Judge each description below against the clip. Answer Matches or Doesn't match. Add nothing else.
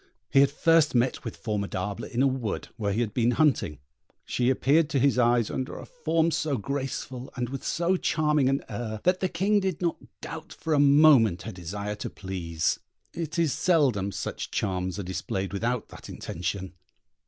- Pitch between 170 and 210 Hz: Doesn't match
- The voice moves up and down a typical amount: Doesn't match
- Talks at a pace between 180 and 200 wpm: Matches